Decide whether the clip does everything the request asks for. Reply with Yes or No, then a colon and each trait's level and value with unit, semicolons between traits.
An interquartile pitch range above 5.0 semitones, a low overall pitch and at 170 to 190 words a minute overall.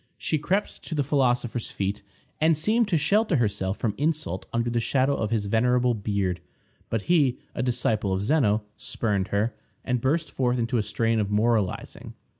Yes: wide, 5.4 semitones; low, 120 Hz; average, 175 wpm